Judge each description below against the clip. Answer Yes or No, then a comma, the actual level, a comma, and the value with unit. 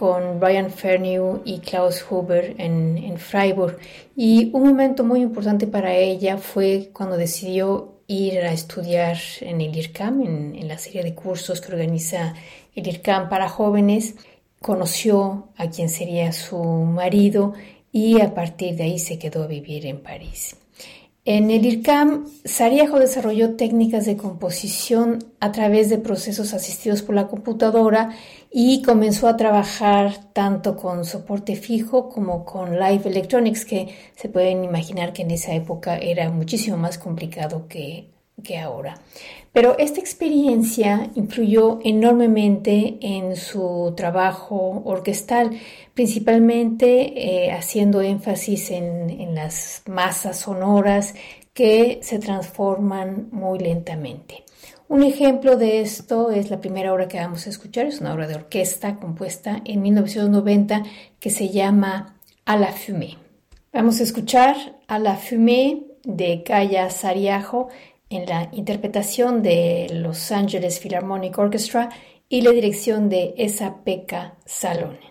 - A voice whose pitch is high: Yes, high, 200 Hz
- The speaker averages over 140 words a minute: No, average, 135 wpm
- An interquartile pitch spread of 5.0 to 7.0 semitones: No, average, 3.8 semitones